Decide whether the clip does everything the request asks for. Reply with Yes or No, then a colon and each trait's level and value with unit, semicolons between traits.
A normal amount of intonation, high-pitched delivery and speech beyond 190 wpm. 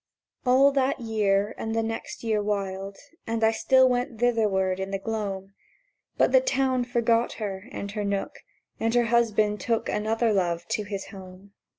No: average, 3.1 semitones; high, 220 Hz; average, 170 wpm